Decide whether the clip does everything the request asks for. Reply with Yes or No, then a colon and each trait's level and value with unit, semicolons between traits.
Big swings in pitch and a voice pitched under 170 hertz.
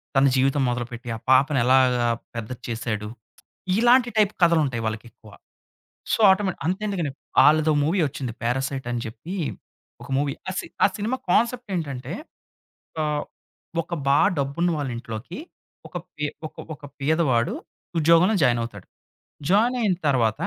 Yes: wide, 6.4 semitones; medium, 140 Hz